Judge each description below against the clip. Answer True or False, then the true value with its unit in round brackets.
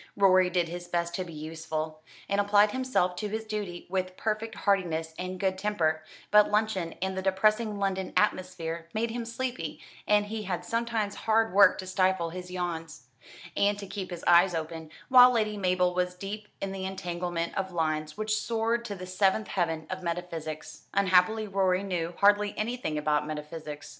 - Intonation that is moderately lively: True (3.5 semitones)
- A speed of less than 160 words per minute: False (175 wpm)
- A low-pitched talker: False (185 Hz)